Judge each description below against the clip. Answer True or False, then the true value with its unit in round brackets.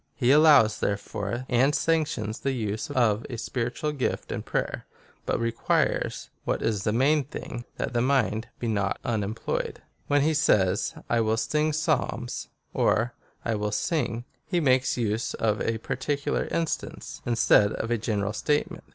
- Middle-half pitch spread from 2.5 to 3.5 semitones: False (4.6 semitones)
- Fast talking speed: False (160 wpm)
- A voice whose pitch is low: True (120 Hz)